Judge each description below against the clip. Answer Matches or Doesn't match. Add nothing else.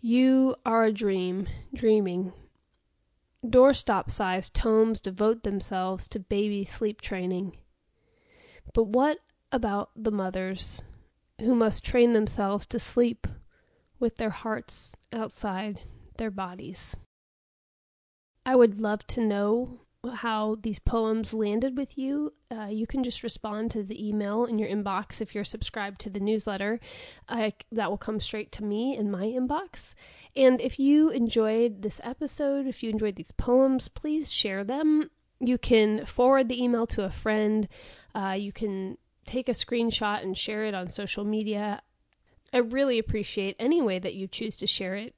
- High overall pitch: Matches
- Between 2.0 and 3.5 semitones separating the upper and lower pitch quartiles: Matches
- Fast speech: Doesn't match